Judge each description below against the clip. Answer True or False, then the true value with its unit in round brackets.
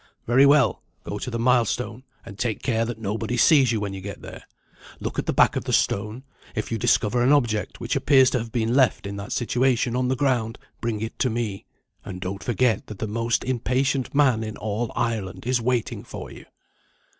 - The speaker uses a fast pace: True (210 wpm)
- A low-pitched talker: True (115 Hz)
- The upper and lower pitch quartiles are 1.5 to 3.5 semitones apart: True (2.7 semitones)